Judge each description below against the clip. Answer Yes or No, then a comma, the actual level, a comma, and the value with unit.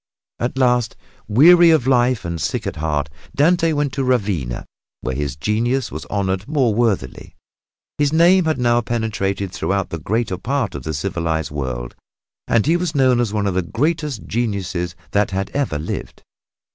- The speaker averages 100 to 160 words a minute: No, average, 170 wpm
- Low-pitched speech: Yes, low, 110 Hz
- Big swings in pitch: Yes, wide, 6.9 semitones